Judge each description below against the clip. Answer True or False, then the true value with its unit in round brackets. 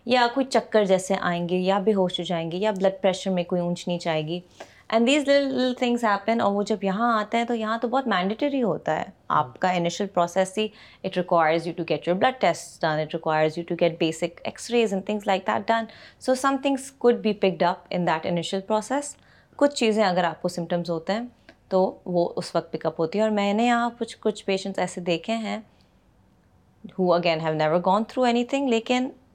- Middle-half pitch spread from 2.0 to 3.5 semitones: False (4.8 semitones)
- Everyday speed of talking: False (230 wpm)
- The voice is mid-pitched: False (195 Hz)